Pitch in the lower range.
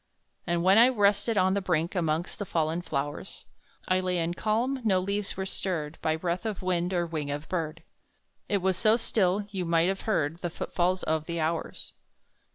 No: medium, 180 Hz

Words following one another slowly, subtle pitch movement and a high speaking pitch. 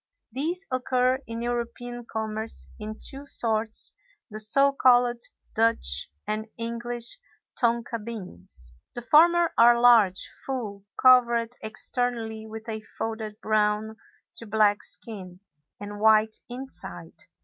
Yes: slow, 115 wpm; narrow, 2.1 semitones; high, 230 Hz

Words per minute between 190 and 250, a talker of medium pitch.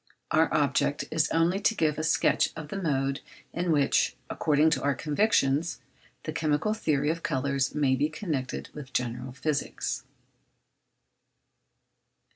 No: slow, 135 wpm; medium, 150 Hz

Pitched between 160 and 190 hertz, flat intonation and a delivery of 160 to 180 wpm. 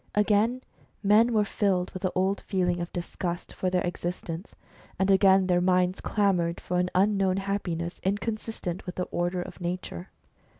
Yes: medium, 185 Hz; narrow, 2.1 semitones; average, 165 wpm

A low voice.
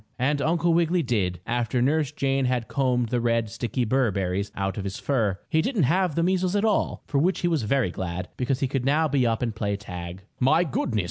Yes: low, 125 Hz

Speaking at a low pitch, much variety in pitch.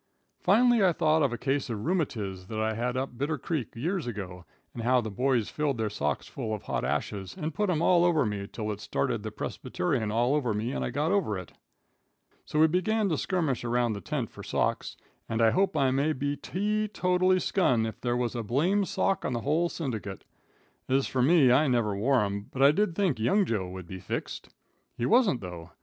Yes: low, 130 Hz; wide, 7.2 semitones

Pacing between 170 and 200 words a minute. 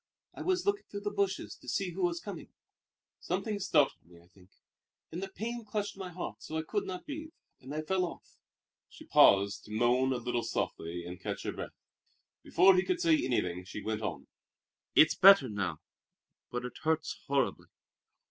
Yes: average, 190 wpm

